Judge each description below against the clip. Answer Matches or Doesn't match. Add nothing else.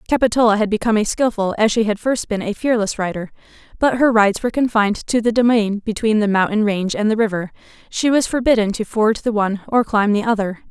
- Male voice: Doesn't match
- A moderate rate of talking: Doesn't match